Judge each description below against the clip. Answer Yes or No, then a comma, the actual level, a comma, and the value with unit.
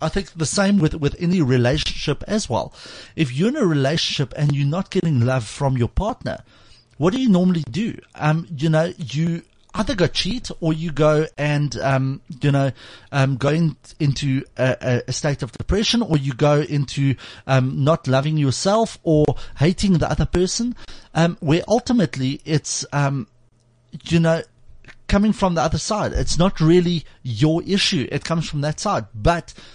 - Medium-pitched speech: Yes, medium, 155 Hz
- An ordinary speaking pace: Yes, average, 175 wpm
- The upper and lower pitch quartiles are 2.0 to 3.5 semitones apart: No, average, 4.2 semitones